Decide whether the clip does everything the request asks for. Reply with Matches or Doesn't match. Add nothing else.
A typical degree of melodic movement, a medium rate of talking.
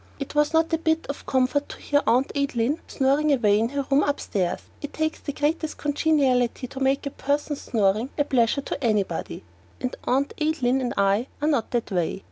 Matches